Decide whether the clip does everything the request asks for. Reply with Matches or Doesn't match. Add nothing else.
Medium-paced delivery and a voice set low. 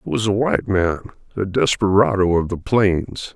Matches